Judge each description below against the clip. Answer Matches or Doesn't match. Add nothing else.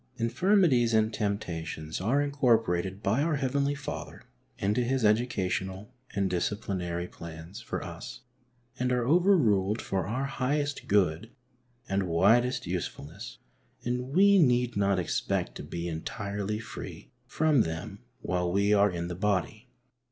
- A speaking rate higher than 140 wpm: Doesn't match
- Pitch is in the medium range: Doesn't match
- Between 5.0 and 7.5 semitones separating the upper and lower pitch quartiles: Matches